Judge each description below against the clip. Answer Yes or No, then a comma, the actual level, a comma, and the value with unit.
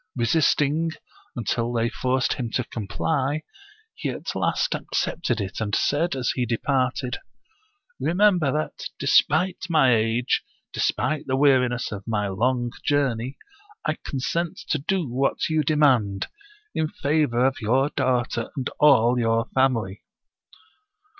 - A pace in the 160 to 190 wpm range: No, slow, 135 wpm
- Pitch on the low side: Yes, low, 130 Hz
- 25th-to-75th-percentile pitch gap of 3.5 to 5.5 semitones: Yes, average, 4.3 semitones